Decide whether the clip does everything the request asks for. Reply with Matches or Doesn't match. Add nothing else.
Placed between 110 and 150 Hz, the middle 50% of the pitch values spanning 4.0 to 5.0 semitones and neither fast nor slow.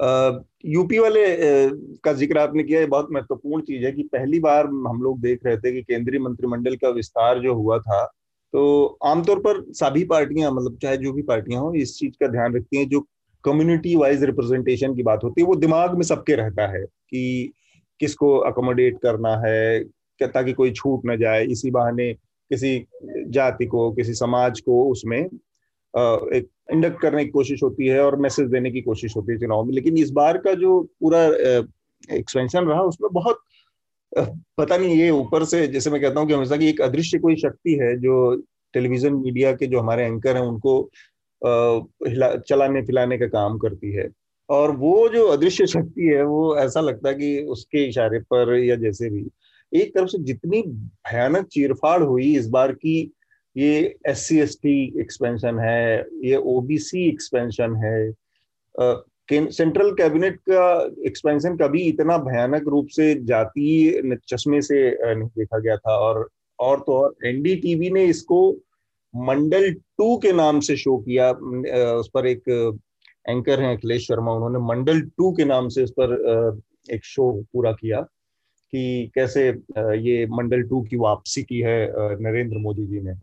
Matches